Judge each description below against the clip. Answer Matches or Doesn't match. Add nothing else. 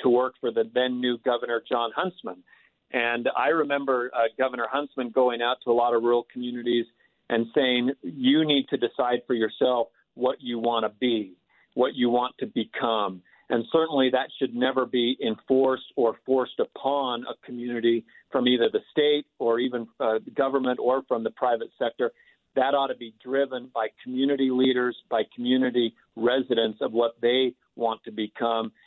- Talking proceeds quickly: Doesn't match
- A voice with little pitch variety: Matches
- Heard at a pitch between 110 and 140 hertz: Matches